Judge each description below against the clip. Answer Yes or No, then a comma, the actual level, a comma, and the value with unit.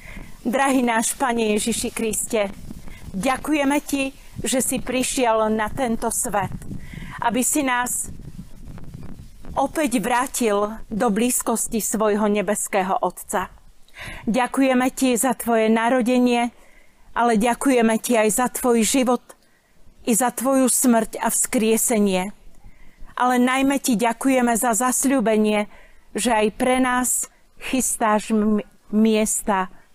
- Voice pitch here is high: Yes, high, 235 Hz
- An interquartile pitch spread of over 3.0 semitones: No, narrow, 2.5 semitones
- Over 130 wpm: No, slow, 110 wpm